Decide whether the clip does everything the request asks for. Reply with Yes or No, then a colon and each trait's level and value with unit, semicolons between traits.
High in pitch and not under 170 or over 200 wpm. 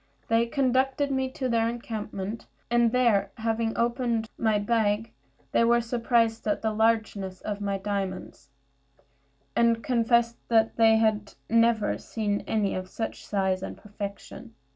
No: high, 225 Hz; average, 140 wpm